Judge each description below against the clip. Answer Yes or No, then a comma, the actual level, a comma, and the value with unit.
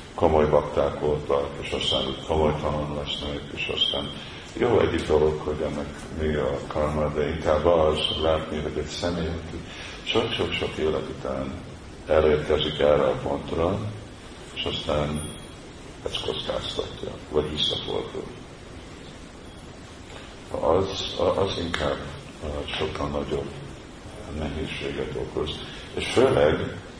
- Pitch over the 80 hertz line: No, very low, 75 Hz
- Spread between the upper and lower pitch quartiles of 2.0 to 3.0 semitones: No, narrow, 1.5 semitones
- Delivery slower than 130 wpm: Yes, slow, 105 wpm